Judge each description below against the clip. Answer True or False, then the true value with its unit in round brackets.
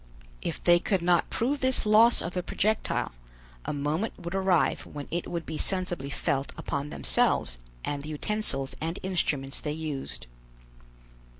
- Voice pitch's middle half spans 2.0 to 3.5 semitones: False (4.8 semitones)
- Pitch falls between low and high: True (170 Hz)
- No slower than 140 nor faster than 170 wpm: True (155 wpm)